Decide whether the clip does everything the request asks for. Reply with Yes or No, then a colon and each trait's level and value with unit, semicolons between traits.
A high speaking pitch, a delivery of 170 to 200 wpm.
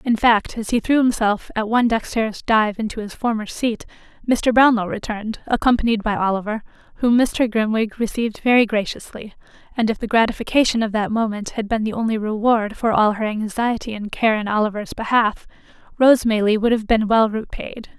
Yes: high, 220 Hz; average, 180 wpm